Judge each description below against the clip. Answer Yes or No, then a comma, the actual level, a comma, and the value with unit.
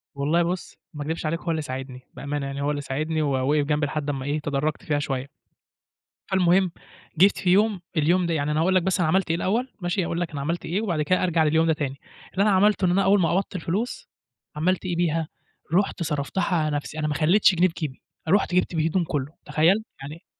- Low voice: No, medium, 165 Hz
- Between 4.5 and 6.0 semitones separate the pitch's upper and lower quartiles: No, average, 3.8 semitones